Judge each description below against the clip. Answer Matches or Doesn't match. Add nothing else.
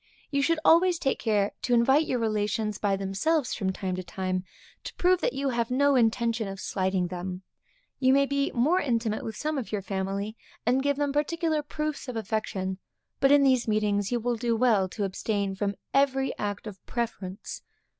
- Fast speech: Doesn't match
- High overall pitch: Matches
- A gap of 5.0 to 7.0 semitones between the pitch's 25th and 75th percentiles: Matches